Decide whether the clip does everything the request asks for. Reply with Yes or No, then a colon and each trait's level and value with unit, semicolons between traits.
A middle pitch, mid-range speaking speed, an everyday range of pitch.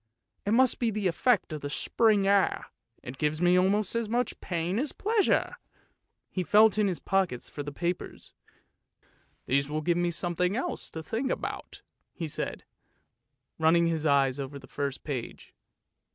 No: medium, 175 Hz; average, 170 wpm; wide, 5.9 semitones